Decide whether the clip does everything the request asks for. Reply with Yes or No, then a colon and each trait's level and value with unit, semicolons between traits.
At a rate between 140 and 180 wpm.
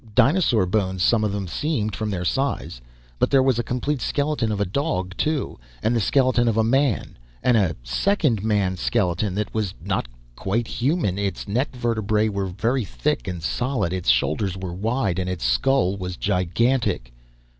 Yes: average, 175 wpm